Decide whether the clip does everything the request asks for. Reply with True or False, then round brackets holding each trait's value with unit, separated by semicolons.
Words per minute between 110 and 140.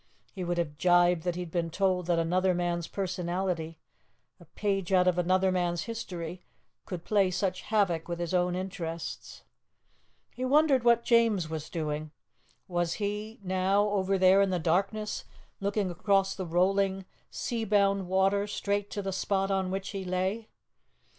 False (160 wpm)